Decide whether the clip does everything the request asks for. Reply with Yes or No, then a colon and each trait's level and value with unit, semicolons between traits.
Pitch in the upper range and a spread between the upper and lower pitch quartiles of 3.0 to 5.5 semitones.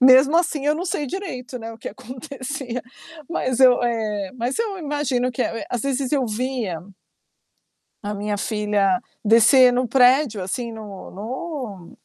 Yes: very high, 250 Hz; average, 3.8 semitones